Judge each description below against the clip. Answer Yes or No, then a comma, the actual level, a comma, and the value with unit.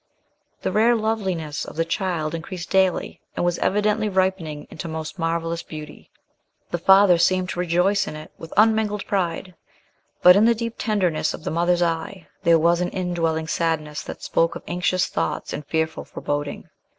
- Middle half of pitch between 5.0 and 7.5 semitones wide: No, average, 2.9 semitones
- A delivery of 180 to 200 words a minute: No, average, 170 wpm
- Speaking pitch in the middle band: Yes, medium, 175 Hz